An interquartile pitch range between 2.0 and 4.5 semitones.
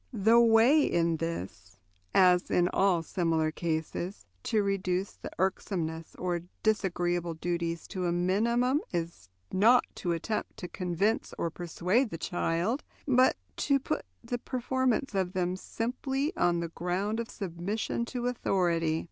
No: average, 4.9 semitones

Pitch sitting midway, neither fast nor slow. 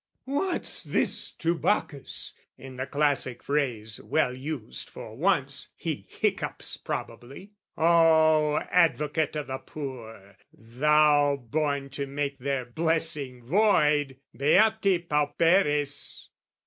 No: medium, 145 Hz; slow, 105 wpm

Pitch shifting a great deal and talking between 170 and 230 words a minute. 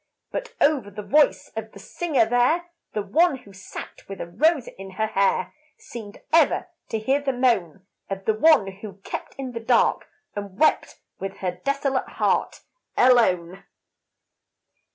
No: wide, 6.1 semitones; average, 155 wpm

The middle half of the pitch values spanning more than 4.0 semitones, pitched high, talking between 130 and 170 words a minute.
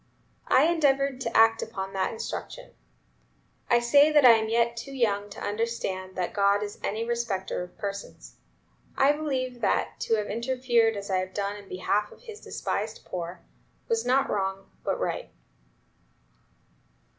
Yes: average, 4.4 semitones; high, 225 Hz; average, 160 wpm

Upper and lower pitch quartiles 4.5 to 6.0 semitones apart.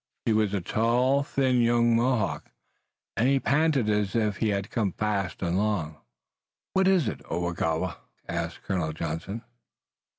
Yes: average, 5.2 semitones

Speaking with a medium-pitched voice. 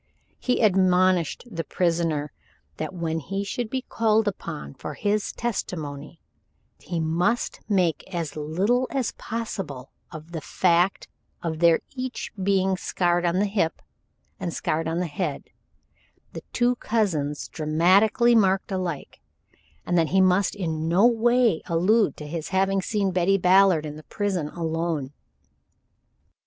Yes: medium, 180 Hz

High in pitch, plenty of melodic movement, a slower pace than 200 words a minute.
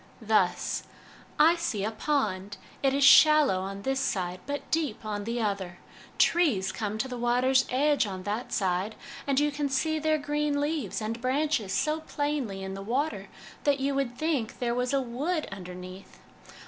Yes: very high, 250 Hz; wide, 6.3 semitones; average, 180 wpm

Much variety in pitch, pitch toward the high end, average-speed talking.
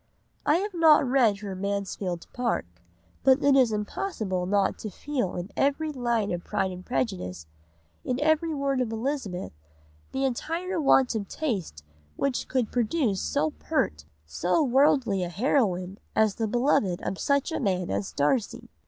Yes: wide, 6.6 semitones; high, 235 Hz; average, 155 wpm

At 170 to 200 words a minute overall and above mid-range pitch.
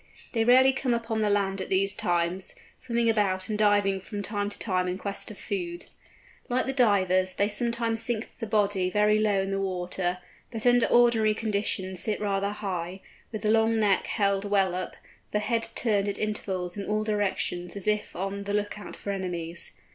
Yes: average, 195 wpm; high, 205 Hz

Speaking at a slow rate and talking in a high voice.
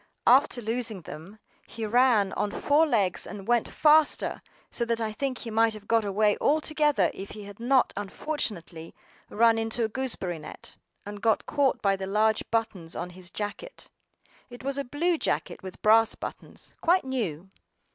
No: average, 170 wpm; high, 225 Hz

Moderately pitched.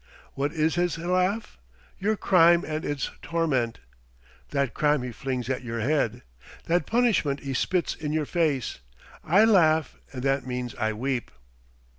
Yes: medium, 150 Hz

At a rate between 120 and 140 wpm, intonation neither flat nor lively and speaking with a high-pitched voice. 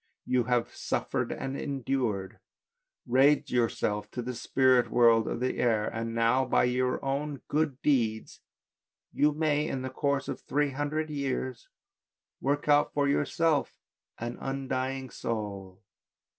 No: slow, 135 wpm; average, 3.2 semitones; low, 130 Hz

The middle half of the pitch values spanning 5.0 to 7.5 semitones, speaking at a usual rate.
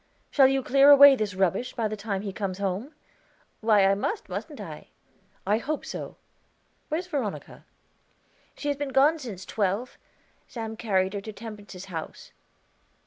Yes: wide, 5.5 semitones; average, 155 wpm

